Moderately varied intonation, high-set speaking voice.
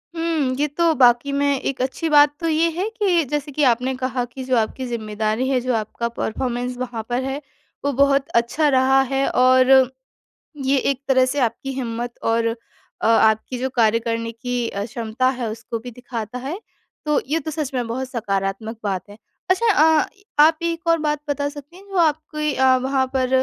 Yes: average, 3.7 semitones; very high, 260 Hz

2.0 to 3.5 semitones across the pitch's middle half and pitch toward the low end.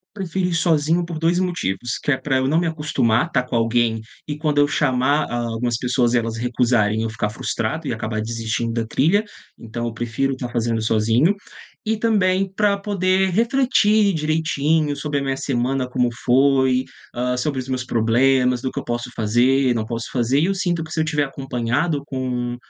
No: average, 5.2 semitones; low, 130 Hz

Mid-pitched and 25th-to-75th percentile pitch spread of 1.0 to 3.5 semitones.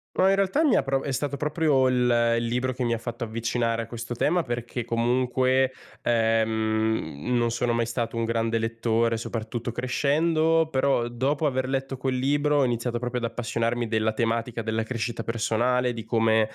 No: low, 120 Hz; narrow, 2.4 semitones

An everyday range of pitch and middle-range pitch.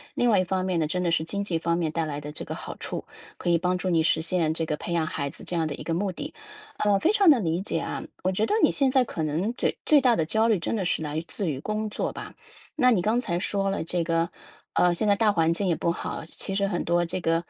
Yes: average, 3.9 semitones; medium, 180 Hz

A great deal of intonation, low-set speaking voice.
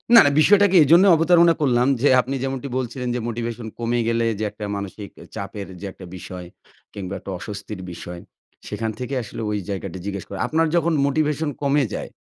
Yes: wide, 6.6 semitones; low, 120 Hz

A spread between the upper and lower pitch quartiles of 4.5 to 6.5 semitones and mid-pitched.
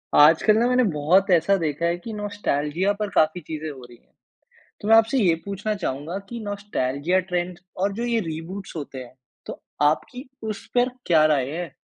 Yes: average, 5.2 semitones; medium, 175 Hz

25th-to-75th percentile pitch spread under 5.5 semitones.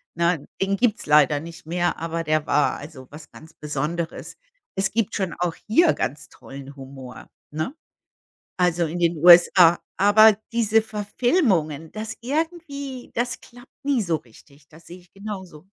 No: wide, 6.0 semitones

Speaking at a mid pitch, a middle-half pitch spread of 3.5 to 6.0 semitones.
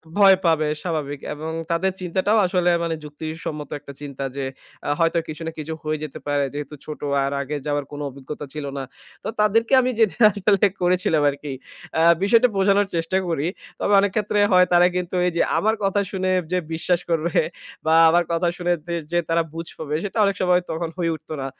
Yes: medium, 170 Hz; average, 3.8 semitones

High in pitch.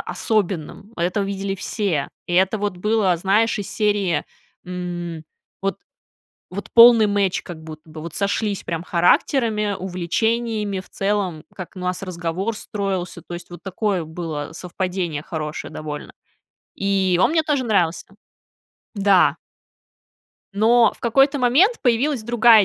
Yes: high, 195 Hz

